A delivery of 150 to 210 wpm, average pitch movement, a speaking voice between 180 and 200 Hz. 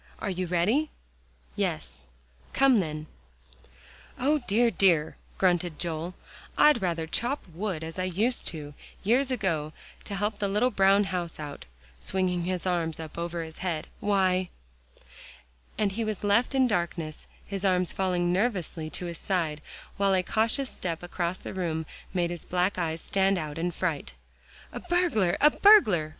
Yes: average, 155 wpm; average, 3.6 semitones; medium, 185 Hz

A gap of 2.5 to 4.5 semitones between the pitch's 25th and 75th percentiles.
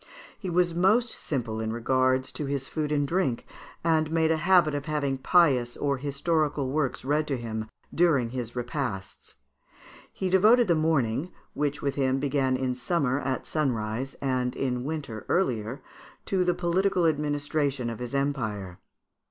Yes: average, 4.2 semitones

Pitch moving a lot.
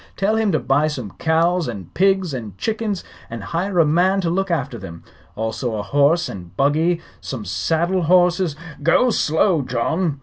Yes: wide, 6.5 semitones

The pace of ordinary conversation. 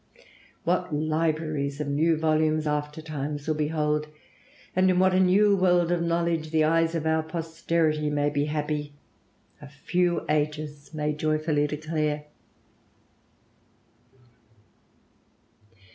No: slow, 115 wpm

